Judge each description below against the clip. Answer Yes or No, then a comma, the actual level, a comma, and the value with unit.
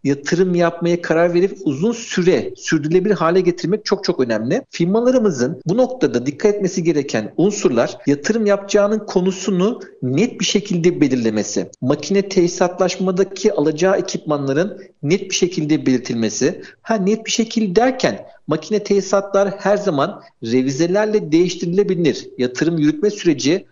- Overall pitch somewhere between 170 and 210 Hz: Yes, medium, 185 Hz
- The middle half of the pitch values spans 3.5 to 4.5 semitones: No, average, 4.9 semitones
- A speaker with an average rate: Yes, average, 120 wpm